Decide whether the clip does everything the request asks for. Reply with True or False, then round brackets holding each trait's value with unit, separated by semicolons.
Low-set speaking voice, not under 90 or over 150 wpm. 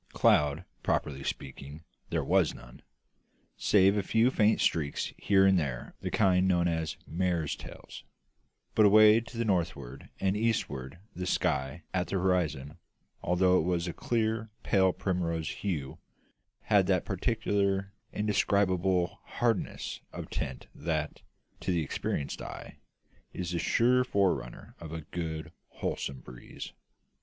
True (90 Hz; 140 wpm)